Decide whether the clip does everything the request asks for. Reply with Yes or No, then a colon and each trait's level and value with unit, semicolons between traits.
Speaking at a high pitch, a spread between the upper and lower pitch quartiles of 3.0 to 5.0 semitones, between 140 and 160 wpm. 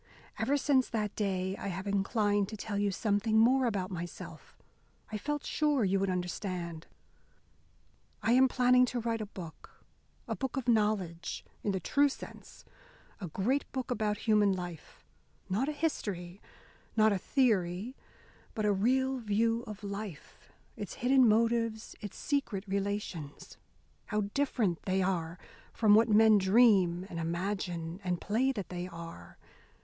Yes: high, 205 Hz; average, 4.1 semitones; average, 150 wpm